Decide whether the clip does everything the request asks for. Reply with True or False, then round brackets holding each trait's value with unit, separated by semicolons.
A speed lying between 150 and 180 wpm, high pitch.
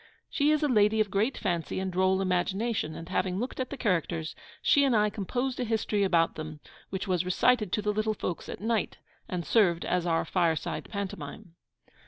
False (195 wpm; 195 Hz)